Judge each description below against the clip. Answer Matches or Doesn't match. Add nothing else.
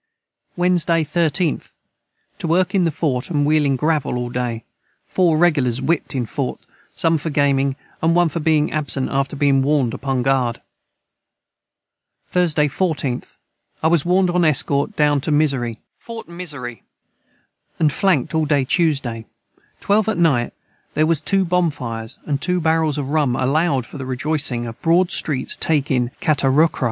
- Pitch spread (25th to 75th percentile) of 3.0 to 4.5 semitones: Matches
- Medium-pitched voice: Matches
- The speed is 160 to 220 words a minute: Doesn't match